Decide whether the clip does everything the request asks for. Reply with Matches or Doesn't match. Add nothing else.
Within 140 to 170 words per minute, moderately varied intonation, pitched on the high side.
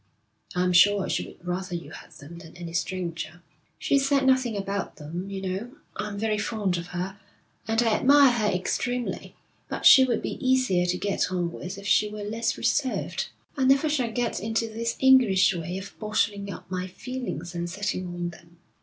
Doesn't match